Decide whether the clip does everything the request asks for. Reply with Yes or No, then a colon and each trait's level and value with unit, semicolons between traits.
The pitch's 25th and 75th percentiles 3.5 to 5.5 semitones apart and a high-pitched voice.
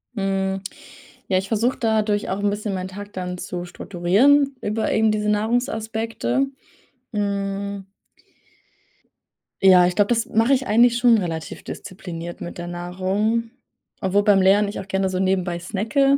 No: average, 2.9 semitones; high, 205 Hz